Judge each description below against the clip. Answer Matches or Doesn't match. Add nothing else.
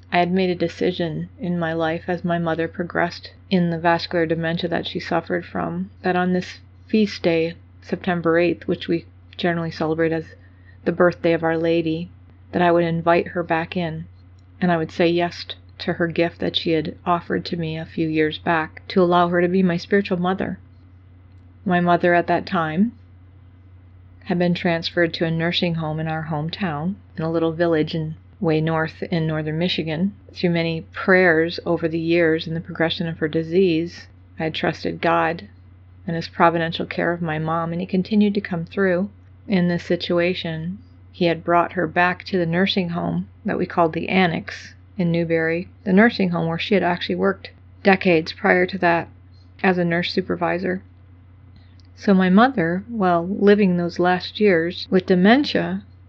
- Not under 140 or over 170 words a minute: Doesn't match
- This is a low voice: Doesn't match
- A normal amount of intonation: Doesn't match